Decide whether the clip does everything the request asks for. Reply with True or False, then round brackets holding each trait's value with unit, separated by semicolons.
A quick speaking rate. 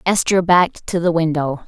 False (180 wpm)